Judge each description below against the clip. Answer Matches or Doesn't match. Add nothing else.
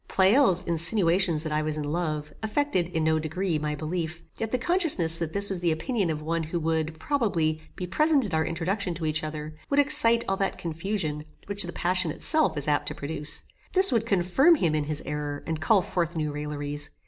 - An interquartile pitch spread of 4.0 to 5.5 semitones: Matches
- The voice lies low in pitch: Doesn't match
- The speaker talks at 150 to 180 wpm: Doesn't match